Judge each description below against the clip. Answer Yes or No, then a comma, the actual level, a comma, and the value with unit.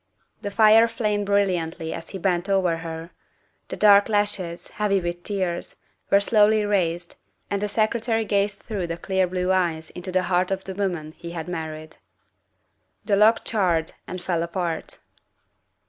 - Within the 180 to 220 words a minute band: No, average, 160 wpm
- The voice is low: No, medium, 185 Hz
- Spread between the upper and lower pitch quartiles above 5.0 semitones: No, average, 3.2 semitones